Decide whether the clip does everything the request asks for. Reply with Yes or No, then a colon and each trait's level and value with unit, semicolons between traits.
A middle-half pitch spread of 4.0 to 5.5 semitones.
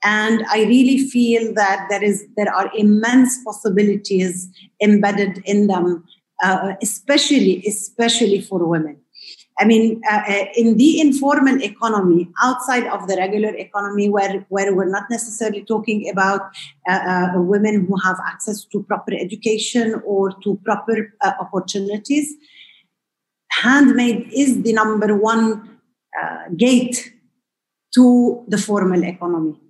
No: average, 2.9 semitones